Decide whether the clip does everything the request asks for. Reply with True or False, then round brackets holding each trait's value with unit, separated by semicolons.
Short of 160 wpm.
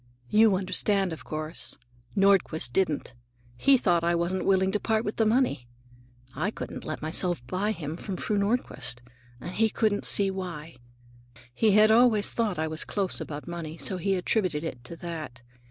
False (170 wpm)